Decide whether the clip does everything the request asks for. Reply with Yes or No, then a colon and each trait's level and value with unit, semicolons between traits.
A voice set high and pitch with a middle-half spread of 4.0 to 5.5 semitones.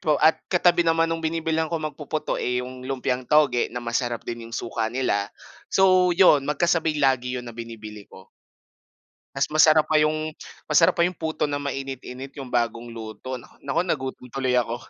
No: low, 135 Hz; average, 4.5 semitones